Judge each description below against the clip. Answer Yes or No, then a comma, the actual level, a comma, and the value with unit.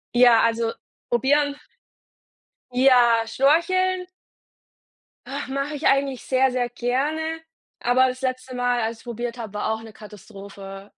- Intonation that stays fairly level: No, average, 3.2 semitones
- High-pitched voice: Yes, high, 245 Hz